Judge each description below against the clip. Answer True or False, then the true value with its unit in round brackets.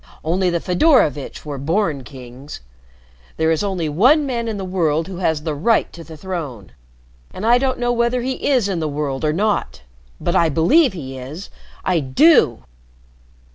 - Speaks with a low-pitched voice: False (170 Hz)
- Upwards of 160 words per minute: True (175 wpm)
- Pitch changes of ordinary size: False (6.7 semitones)